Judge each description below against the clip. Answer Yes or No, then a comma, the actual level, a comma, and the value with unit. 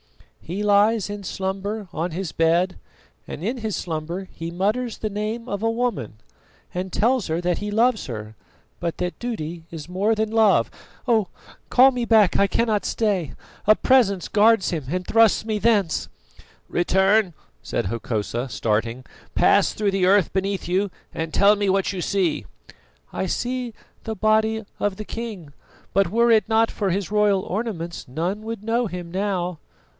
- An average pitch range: Yes, average, 4.0 semitones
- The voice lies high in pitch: Yes, high, 200 Hz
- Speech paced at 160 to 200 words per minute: Yes, average, 165 wpm